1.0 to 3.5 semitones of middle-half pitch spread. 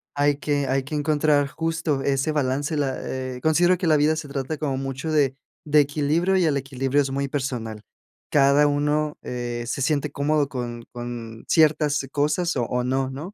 Yes: narrow, 2.4 semitones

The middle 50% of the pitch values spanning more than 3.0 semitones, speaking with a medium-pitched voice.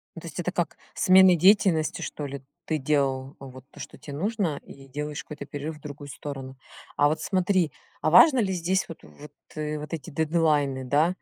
Yes: average, 3.6 semitones; medium, 150 Hz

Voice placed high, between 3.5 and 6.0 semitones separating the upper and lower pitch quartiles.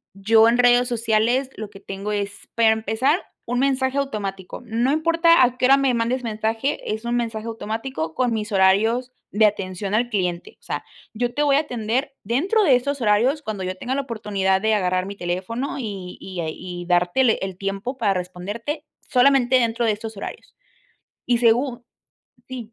Yes: high, 225 Hz; average, 4.2 semitones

